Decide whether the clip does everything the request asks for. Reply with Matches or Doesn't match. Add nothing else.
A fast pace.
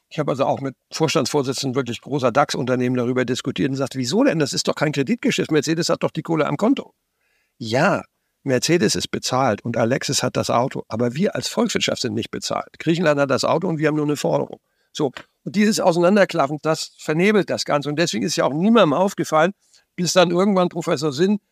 Matches